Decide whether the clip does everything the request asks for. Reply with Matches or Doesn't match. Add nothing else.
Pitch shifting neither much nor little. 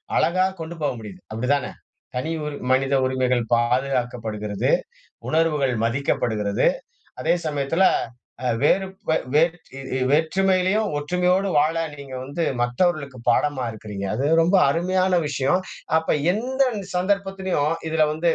Doesn't match